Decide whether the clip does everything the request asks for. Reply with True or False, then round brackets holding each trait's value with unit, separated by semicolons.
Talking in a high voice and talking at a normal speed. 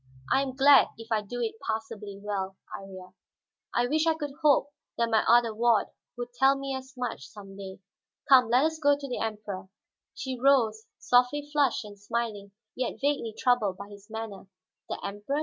True (235 Hz; 185 wpm)